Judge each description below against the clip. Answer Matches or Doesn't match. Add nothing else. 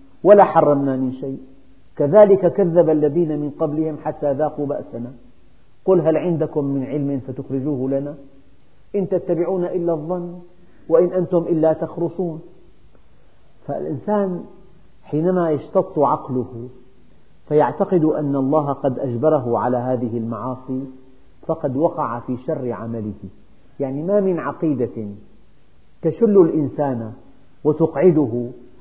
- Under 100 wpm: Doesn't match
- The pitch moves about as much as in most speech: Matches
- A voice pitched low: Doesn't match